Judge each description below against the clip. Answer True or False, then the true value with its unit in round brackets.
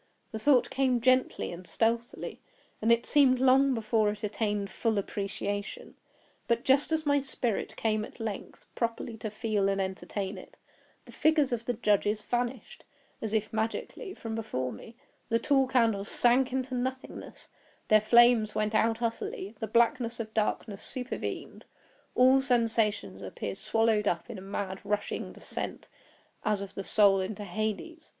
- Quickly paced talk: False (155 wpm)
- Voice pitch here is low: False (225 Hz)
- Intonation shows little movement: False (3.1 semitones)